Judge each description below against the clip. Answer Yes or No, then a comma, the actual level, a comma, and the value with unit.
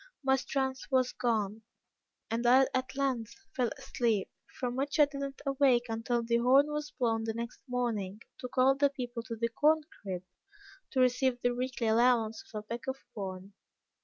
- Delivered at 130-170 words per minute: No, average, 180 wpm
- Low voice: No, high, 245 Hz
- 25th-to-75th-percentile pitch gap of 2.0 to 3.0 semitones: Yes, average, 2.7 semitones